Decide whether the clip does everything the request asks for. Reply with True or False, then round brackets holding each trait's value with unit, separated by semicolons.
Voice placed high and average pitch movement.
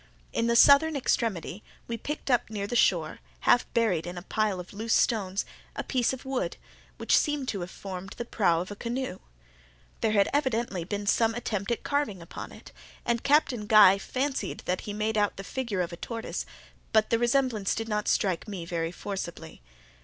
True (215 Hz; 4.0 semitones)